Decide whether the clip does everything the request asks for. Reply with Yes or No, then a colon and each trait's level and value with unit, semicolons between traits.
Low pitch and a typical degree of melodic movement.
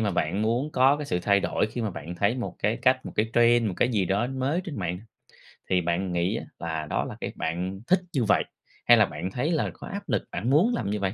No: low, 105 Hz; wide, 5.9 semitones